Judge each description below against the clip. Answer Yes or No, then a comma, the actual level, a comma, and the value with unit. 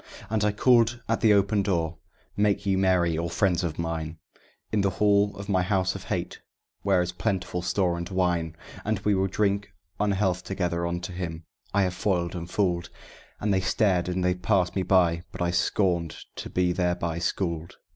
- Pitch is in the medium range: No, very low, 90 Hz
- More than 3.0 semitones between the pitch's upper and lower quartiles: No, narrow, 2.5 semitones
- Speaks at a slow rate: No, average, 185 wpm